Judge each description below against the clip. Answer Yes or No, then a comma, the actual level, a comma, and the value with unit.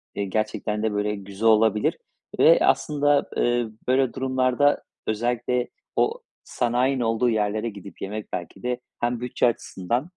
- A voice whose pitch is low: Yes, low, 115 Hz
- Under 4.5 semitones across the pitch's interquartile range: Yes, average, 2.9 semitones